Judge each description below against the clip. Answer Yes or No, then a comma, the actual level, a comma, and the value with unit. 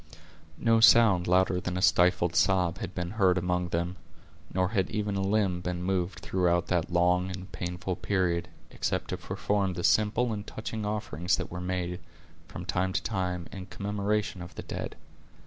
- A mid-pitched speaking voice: No, very low, 90 Hz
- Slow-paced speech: No, average, 175 wpm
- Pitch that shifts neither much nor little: No, narrow, 2.1 semitones